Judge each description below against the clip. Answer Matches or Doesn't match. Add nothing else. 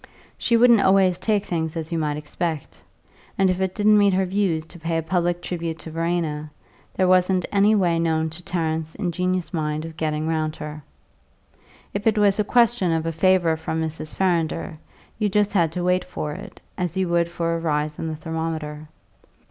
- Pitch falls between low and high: Matches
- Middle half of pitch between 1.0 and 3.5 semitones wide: Matches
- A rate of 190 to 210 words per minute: Matches